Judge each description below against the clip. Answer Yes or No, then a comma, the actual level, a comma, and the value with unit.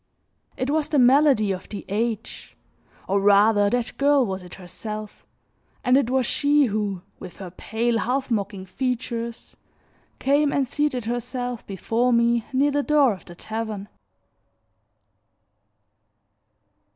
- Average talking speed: No, slow, 130 wpm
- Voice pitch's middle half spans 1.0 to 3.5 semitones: No, average, 4.3 semitones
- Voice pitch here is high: Yes, high, 235 Hz